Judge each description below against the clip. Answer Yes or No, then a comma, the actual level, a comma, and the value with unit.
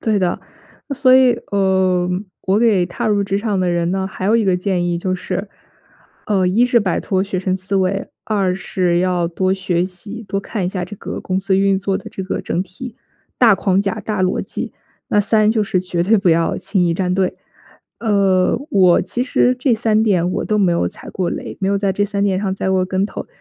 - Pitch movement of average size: No, narrow, 2.1 semitones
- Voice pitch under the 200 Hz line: Yes, high, 190 Hz